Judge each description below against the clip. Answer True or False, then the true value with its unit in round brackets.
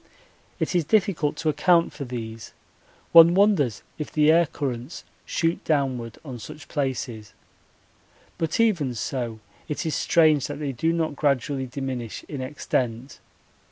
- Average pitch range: True (4.6 semitones)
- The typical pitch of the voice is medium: True (145 Hz)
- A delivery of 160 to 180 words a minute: False (140 wpm)